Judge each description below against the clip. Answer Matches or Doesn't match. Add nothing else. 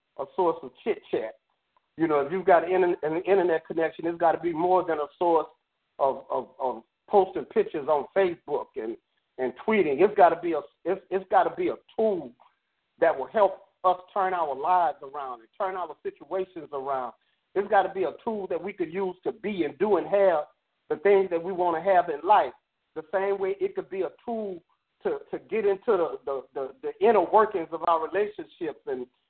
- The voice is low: Doesn't match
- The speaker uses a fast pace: Matches